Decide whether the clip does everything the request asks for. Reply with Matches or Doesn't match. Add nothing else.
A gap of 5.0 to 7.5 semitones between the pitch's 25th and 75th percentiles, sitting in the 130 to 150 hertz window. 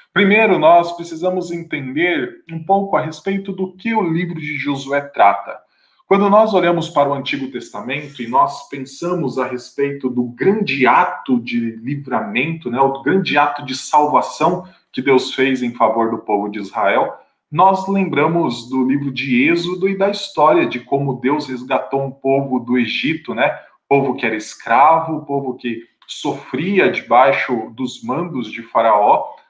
Matches